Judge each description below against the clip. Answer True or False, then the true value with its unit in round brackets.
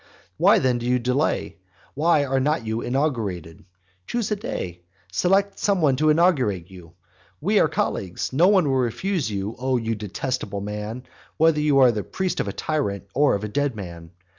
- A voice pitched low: True (125 Hz)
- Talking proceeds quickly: False (180 wpm)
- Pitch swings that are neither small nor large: False (6.8 semitones)